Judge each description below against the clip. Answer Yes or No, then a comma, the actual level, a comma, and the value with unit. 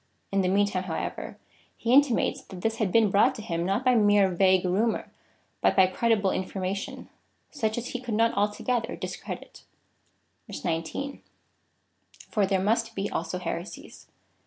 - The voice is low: No, high, 200 Hz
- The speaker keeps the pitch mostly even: No, average, 3.5 semitones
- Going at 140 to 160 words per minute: Yes, average, 155 wpm